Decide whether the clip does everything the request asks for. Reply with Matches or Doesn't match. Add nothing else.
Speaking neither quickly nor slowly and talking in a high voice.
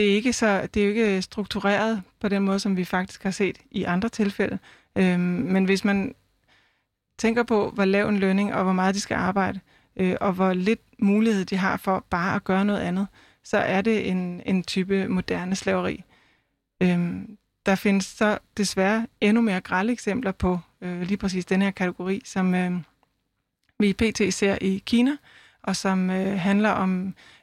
Matches